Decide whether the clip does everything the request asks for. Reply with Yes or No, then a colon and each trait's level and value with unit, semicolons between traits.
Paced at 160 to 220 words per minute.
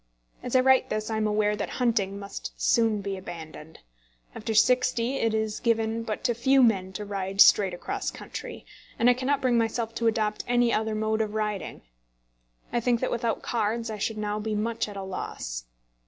Yes: average, 195 wpm